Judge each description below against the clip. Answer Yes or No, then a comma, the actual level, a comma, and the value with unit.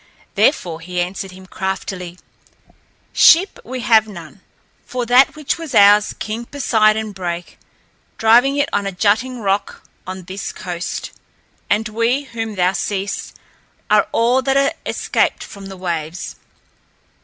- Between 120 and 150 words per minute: Yes, slow, 135 wpm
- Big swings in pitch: No, average, 4.5 semitones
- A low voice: No, high, 205 Hz